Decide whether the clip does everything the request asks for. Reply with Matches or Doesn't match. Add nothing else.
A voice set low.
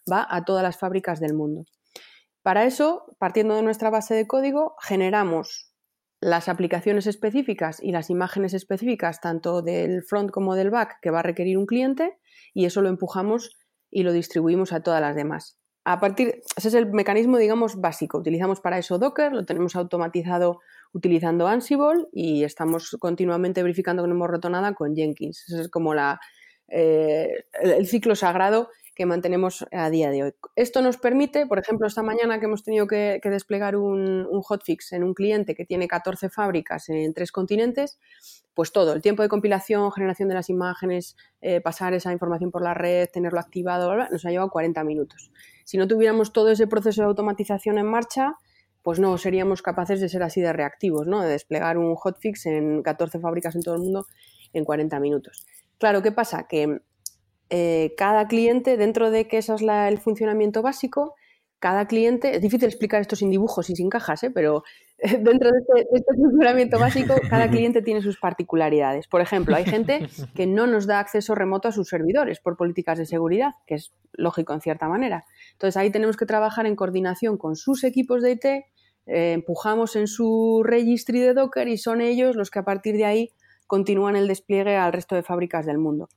Doesn't match